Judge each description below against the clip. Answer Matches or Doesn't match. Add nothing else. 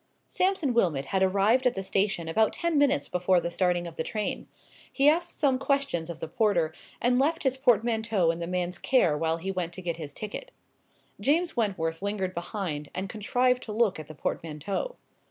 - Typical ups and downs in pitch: Doesn't match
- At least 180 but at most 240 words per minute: Matches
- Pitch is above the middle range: Matches